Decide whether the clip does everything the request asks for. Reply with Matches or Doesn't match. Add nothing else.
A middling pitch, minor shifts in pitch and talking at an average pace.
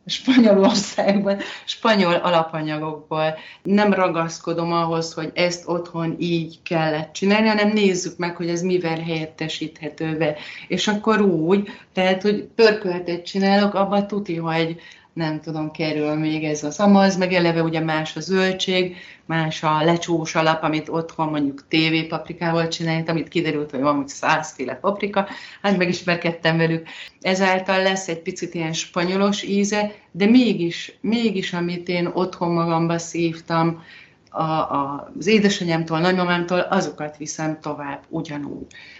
Doesn't match